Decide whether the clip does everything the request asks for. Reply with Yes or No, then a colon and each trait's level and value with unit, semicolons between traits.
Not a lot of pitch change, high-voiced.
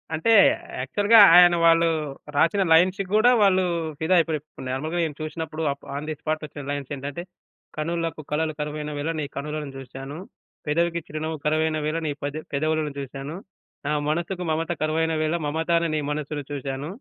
No: narrow, 2.2 semitones; medium, 155 Hz